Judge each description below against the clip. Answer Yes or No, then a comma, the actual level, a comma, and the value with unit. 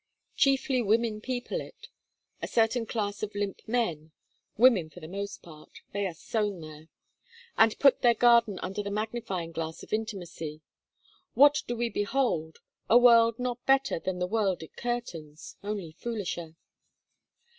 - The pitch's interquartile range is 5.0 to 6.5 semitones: Yes, average, 5.3 semitones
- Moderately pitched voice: No, high, 210 Hz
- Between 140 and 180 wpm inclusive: Yes, average, 150 wpm